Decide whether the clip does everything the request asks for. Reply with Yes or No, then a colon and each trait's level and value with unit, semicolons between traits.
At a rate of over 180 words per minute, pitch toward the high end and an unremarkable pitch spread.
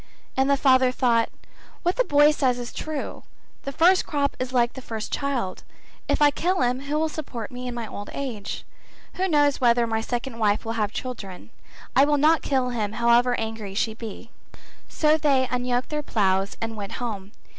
Yes: average, 190 wpm; very high, 250 Hz; average, 4.0 semitones